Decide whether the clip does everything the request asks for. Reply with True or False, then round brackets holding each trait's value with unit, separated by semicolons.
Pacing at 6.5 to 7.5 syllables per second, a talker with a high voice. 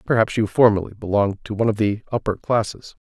False (6.6 syllables/s; 105 Hz)